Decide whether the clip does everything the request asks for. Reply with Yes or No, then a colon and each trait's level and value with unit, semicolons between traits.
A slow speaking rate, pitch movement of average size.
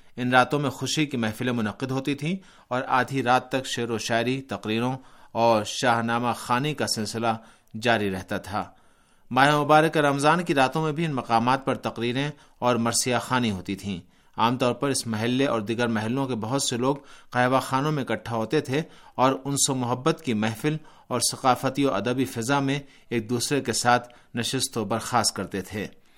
No: average, 185 wpm; average, 3.1 semitones